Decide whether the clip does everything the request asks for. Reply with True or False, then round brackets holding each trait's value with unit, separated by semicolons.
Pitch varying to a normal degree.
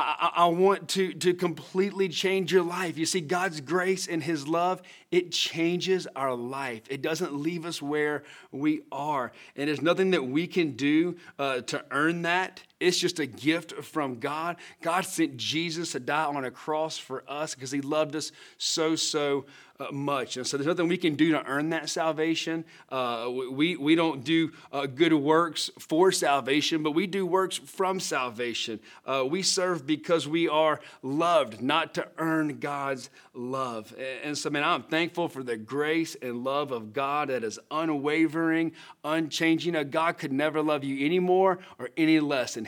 True (3.4 semitones)